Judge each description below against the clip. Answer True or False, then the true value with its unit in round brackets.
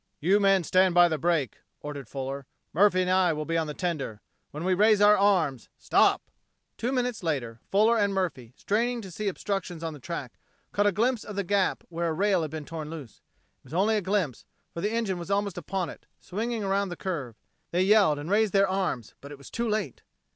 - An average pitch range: True (4.6 semitones)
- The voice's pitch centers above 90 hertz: True (185 Hz)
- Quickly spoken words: True (220 wpm)